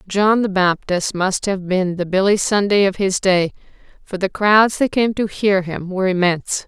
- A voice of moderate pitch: No, high, 195 Hz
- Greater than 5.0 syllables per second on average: No, 4.7 syllables/s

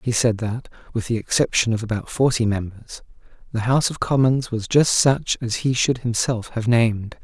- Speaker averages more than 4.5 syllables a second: Yes, 5.0 syllables/s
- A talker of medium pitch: No, low, 120 Hz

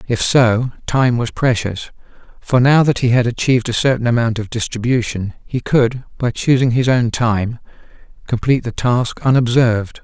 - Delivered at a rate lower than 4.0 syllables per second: No, 4.9 syllables/s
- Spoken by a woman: No, male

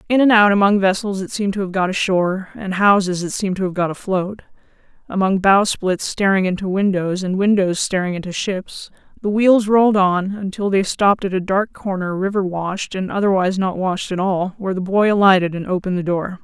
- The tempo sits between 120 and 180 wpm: No, average, 200 wpm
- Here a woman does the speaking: Yes, female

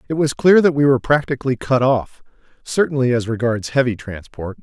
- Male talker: Yes, male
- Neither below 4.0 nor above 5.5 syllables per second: No, 5.7 syllables/s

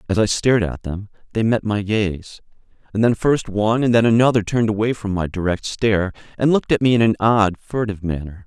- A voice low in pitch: Yes, low, 105 Hz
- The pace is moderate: No, fast, 220 wpm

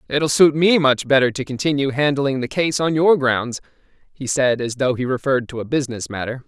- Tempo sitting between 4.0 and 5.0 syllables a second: No, 5.6 syllables/s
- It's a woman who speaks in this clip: No, male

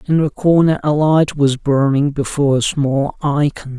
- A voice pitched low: No, medium, 145 Hz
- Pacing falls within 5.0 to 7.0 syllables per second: No, 4.6 syllables/s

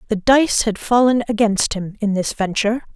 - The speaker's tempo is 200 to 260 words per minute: No, average, 185 wpm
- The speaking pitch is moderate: No, high, 220 Hz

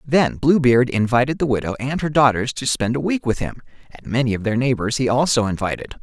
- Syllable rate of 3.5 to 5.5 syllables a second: No, 5.7 syllables/s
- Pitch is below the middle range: Yes, low, 125 Hz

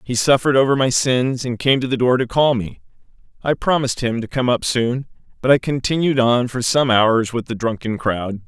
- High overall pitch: No, low, 125 Hz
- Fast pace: Yes, fast, 220 wpm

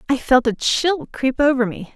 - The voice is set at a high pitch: Yes, very high, 260 Hz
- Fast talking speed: Yes, fast, 215 wpm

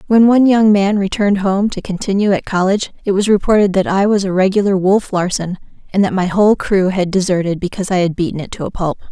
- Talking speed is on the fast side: Yes, fast, 230 wpm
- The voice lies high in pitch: Yes, high, 195 Hz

